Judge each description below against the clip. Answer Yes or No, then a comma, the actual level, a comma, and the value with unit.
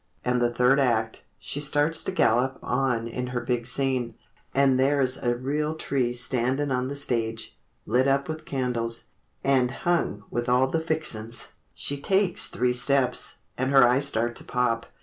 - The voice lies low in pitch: Yes, low, 130 Hz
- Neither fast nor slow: Yes, average, 165 wpm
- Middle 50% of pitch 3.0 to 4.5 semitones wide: No, narrow, 2.4 semitones